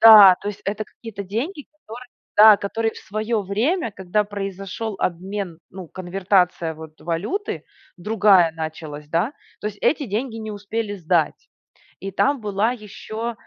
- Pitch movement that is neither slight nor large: Yes, average, 3.5 semitones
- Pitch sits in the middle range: No, high, 205 Hz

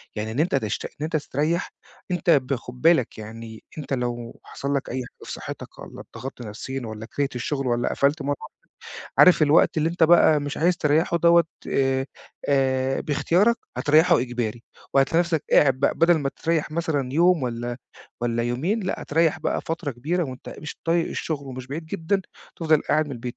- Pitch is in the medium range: Yes, medium, 145 Hz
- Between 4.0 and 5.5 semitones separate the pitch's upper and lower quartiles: Yes, average, 4.7 semitones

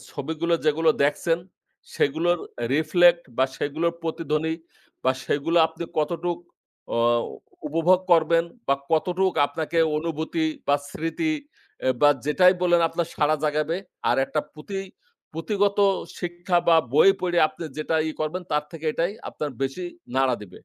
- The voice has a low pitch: No, medium, 165 Hz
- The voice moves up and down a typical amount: No, narrow, 2.3 semitones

